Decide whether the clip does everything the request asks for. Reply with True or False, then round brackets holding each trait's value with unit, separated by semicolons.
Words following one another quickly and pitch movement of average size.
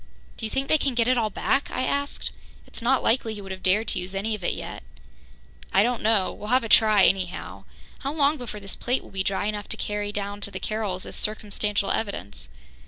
True (235 wpm; 3.5 semitones)